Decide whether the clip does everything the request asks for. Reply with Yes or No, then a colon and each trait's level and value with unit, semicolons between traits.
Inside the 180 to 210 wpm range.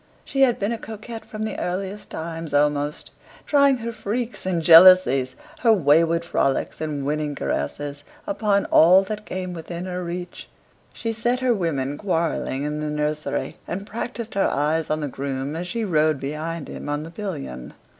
No: average, 170 wpm